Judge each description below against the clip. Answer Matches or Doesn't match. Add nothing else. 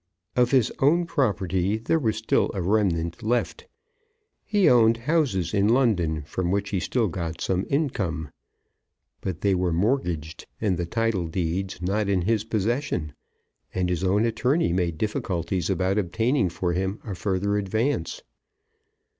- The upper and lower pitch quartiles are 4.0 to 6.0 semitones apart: Matches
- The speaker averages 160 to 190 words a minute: Doesn't match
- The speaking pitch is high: Doesn't match